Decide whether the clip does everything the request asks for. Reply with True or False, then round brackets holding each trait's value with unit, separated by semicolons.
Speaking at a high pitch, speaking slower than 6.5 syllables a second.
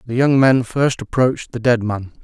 False (125 Hz; 5.0 syllables/s)